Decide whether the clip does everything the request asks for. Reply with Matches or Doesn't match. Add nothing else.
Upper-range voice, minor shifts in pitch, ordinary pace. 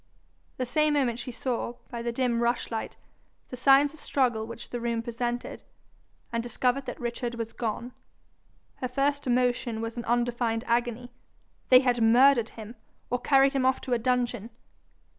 Matches